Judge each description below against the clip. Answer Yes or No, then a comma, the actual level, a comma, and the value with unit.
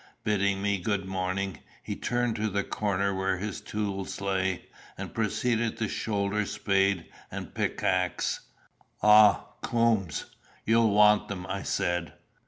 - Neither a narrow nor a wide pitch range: No, narrow, 1.8 semitones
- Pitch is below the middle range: Yes, low, 100 Hz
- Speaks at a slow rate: Yes, slow, 130 wpm